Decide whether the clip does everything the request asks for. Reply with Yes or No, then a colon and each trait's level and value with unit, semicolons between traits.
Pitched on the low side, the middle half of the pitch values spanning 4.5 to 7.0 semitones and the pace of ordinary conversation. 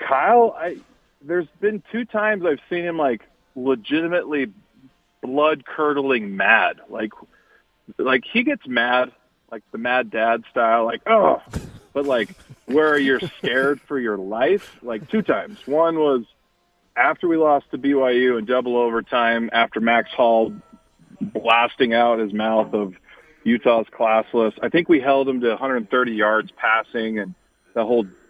Yes: low, 125 Hz; average, 5.1 semitones; average, 150 wpm